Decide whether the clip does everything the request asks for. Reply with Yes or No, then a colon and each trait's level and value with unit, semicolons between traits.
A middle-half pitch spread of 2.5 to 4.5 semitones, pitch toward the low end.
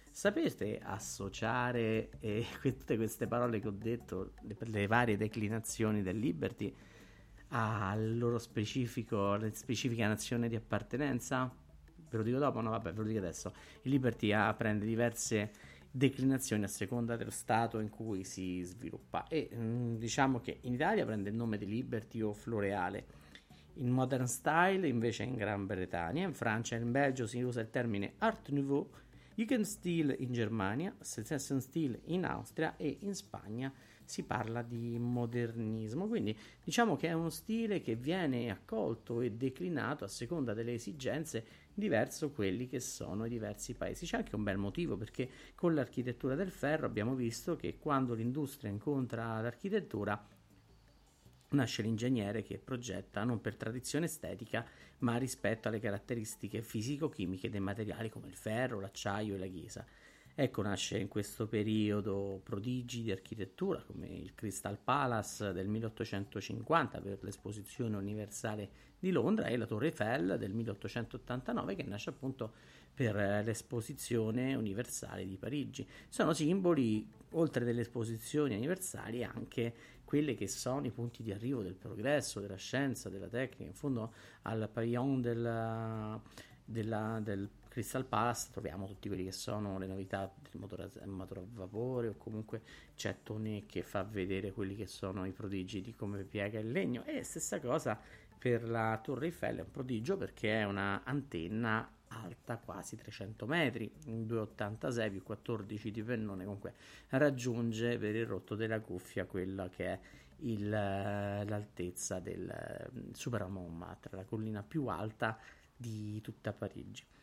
Yes: average, 3.4 semitones; low, 115 Hz